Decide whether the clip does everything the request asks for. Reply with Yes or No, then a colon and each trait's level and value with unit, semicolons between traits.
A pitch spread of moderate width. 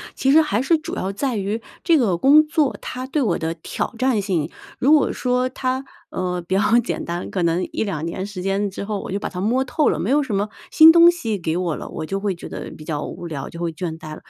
No: wide, 7.1 semitones